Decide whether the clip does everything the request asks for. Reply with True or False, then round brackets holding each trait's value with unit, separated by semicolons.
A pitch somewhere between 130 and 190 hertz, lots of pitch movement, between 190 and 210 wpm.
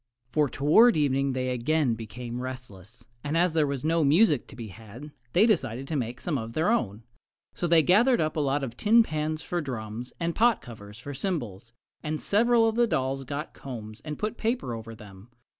True (140 Hz; 6.0 semitones; 200 wpm)